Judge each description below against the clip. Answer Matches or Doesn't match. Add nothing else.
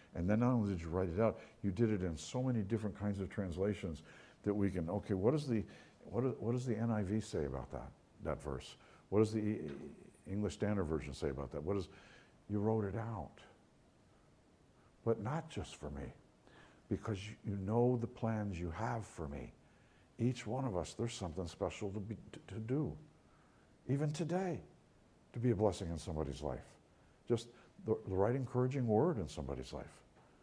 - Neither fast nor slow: Matches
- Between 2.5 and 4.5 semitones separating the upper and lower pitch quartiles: Doesn't match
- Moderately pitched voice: Doesn't match